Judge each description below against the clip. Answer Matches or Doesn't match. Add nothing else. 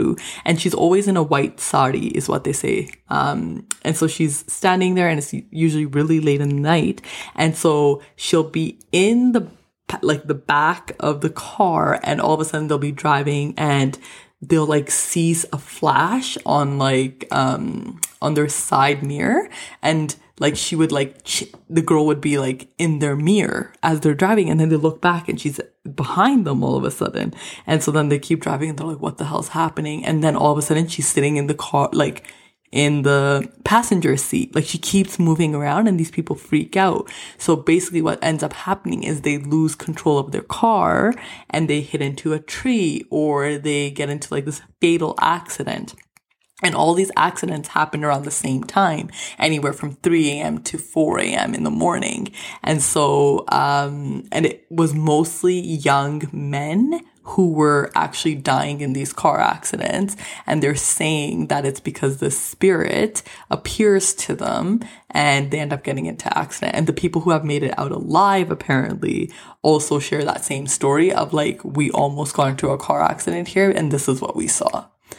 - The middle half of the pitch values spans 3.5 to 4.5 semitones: Doesn't match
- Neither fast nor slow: Matches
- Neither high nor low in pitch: Matches